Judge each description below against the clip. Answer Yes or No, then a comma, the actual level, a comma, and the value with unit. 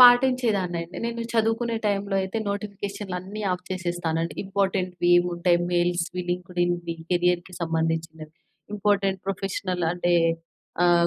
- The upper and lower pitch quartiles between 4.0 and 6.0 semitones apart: No, narrow, 2.5 semitones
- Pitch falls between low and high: Yes, medium, 180 Hz